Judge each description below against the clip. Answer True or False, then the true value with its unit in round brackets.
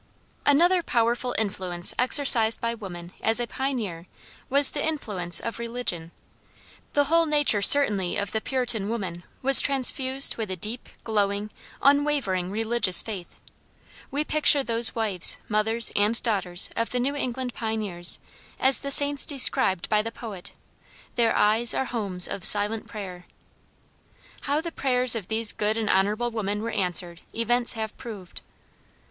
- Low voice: False (225 Hz)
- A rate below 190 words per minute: True (145 wpm)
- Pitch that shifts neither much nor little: True (4.3 semitones)